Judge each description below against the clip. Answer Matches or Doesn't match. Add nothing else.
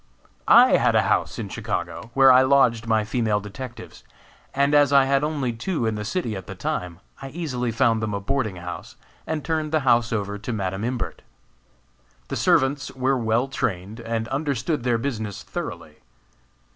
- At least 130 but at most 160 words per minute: Doesn't match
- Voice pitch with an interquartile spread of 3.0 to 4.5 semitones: Matches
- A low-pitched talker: Matches